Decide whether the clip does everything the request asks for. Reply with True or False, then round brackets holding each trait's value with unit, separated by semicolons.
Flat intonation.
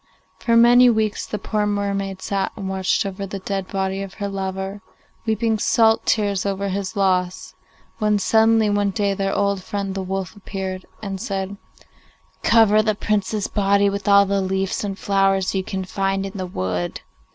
True (1.3 semitones)